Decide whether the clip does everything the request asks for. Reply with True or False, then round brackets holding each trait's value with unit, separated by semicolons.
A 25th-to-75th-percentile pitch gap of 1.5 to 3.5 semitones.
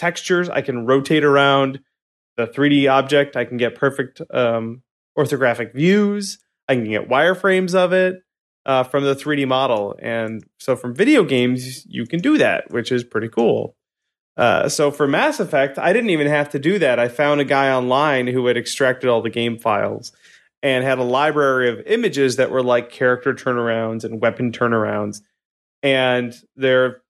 True (3.2 semitones)